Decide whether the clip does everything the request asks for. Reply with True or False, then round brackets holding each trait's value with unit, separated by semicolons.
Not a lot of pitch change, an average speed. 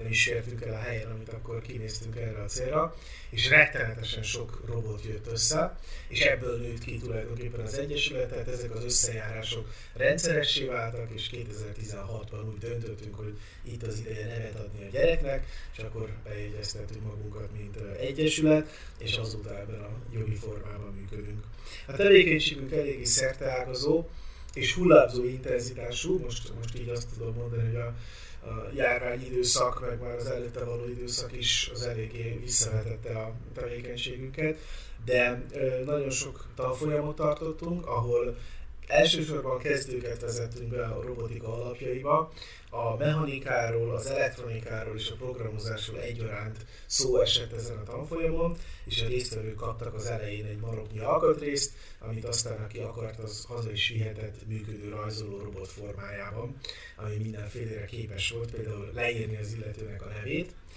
True (2.3 semitones; 140 wpm)